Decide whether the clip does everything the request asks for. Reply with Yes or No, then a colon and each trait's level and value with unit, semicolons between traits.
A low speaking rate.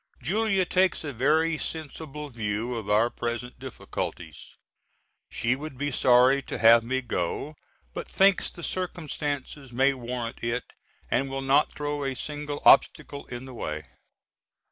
No: average, 145 wpm